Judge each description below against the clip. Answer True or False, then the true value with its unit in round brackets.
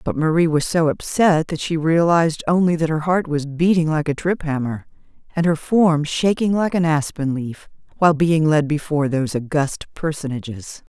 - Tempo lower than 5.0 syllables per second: False (5.1 syllables/s)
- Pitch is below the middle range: False (155 Hz)